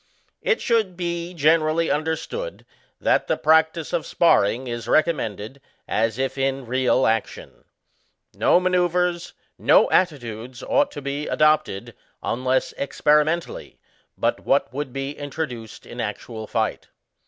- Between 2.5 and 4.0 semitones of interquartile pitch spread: No, average, 5.1 semitones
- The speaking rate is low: Yes, slow, 120 wpm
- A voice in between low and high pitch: Yes, medium, 145 Hz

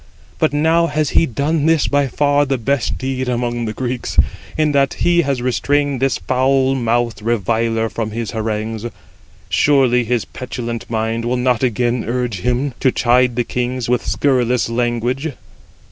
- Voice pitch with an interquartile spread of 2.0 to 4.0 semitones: Yes, average, 2.8 semitones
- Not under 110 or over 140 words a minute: No, average, 160 wpm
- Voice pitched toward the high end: No, low, 125 Hz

